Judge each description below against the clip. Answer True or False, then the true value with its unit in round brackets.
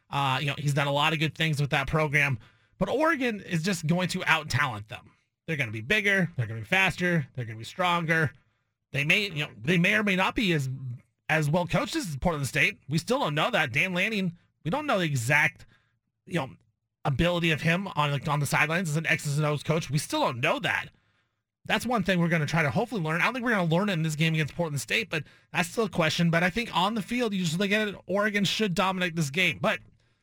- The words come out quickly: True (255 wpm)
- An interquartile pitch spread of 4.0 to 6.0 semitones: True (4.4 semitones)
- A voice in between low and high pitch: True (160 Hz)